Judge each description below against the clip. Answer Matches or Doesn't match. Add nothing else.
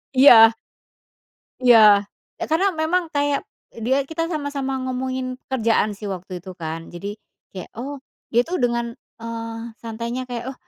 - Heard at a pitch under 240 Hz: Doesn't match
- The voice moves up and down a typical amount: Matches